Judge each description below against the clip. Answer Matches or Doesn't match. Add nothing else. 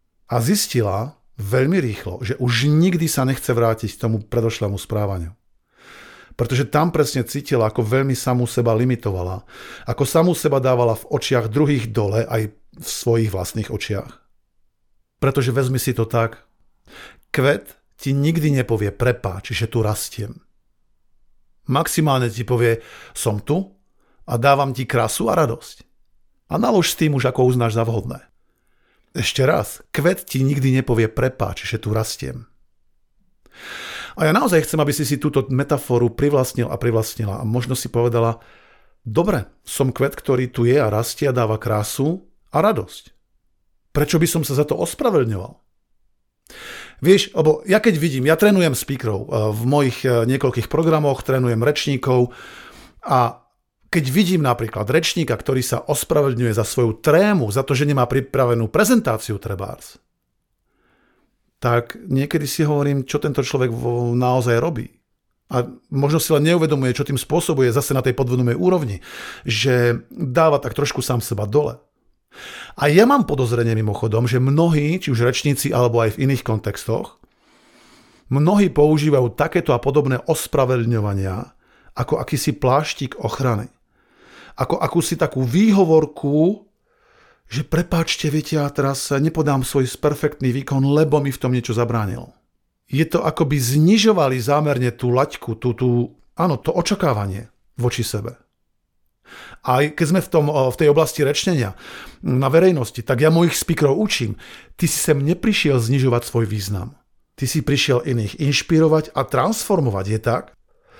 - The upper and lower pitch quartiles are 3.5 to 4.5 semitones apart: Matches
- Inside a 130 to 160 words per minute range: Matches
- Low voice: Matches